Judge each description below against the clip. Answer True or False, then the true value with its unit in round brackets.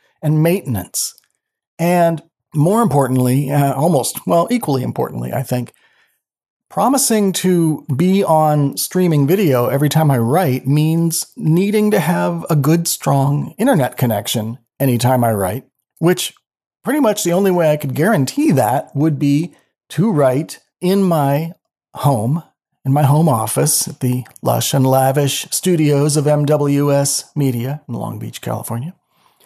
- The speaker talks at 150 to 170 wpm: False (140 wpm)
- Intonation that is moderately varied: True (4.2 semitones)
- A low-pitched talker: False (150 Hz)